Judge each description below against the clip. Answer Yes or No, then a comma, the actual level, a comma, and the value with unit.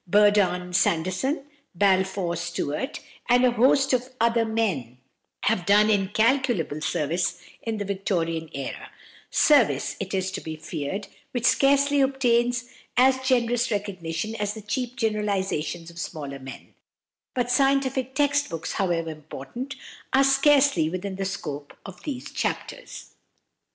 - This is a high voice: Yes, high, 205 Hz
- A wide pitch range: Yes, wide, 6.6 semitones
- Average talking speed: No, slow, 130 wpm